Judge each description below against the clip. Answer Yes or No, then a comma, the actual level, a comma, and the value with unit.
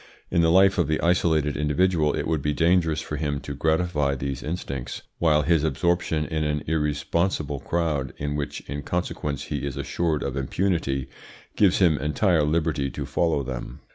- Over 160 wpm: Yes, average, 170 wpm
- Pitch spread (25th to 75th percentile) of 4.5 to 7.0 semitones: No, average, 3.0 semitones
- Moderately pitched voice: No, very low, 75 Hz